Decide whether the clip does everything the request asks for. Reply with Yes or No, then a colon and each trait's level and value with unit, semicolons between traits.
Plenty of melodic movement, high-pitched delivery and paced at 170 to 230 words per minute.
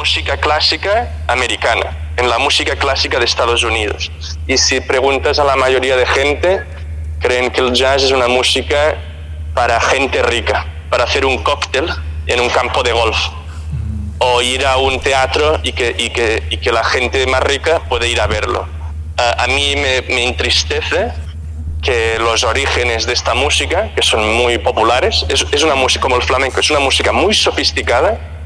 No: wide, 6.9 semitones; very low, 80 Hz; average, 175 wpm